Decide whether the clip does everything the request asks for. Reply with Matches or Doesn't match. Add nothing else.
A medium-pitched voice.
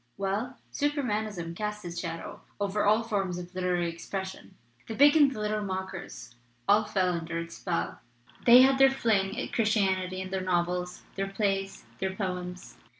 Doesn't match